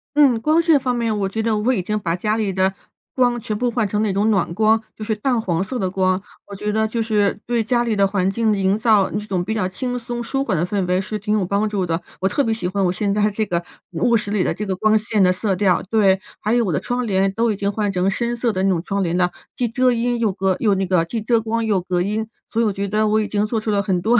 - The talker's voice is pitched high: Yes, high, 210 Hz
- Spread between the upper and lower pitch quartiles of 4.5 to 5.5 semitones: No, average, 2.9 semitones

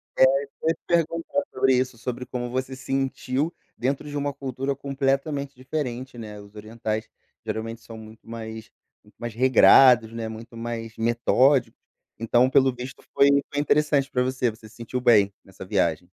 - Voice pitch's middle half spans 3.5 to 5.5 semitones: No, average, 3.1 semitones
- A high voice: No, low, 125 Hz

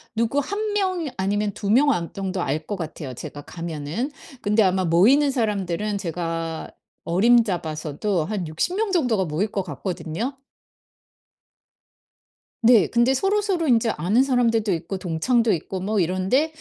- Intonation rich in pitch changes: Yes, wide, 6.5 semitones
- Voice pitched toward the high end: Yes, high, 205 Hz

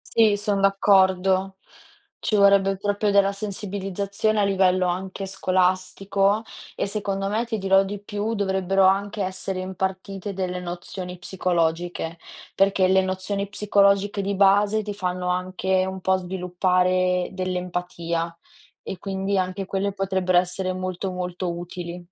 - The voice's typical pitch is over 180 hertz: Yes, high, 190 Hz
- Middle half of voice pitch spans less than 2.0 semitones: Yes, narrow, 1.4 semitones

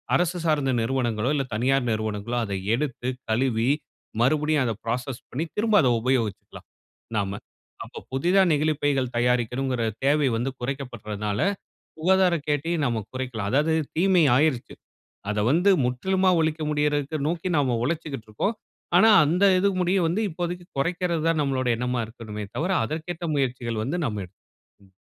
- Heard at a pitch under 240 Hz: Yes, low, 135 Hz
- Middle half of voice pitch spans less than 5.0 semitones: No, average, 5.3 semitones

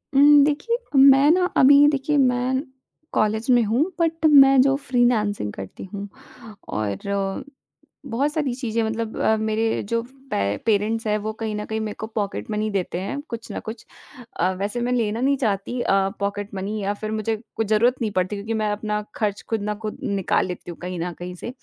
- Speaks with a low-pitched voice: No, high, 220 Hz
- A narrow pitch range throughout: No, average, 3.9 semitones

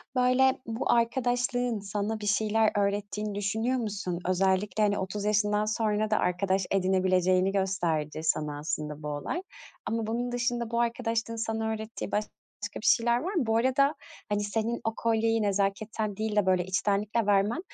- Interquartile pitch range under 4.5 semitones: Yes, average, 2.8 semitones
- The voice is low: No, high, 210 Hz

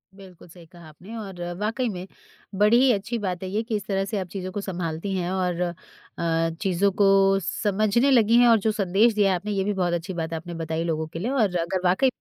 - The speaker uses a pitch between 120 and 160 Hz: No, high, 195 Hz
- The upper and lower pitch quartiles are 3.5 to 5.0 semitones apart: No, average, 3.1 semitones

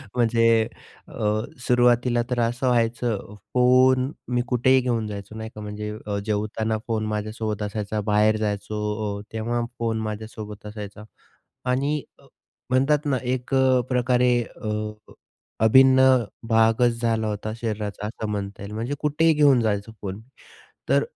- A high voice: No, low, 115 Hz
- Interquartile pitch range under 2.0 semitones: No, average, 2.8 semitones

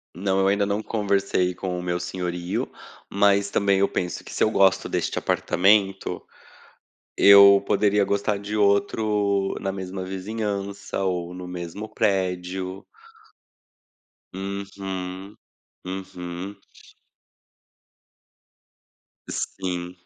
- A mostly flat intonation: Yes, narrow, 1.6 semitones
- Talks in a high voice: No, very low, 95 Hz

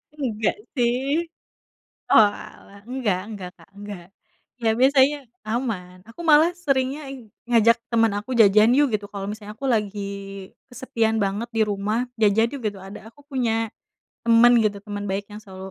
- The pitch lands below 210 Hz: No, high, 220 Hz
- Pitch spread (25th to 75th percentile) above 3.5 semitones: No, average, 3.2 semitones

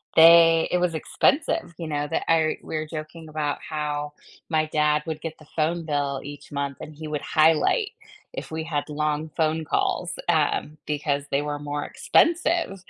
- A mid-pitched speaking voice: Yes, medium, 155 Hz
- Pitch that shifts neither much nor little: No, narrow, 1.8 semitones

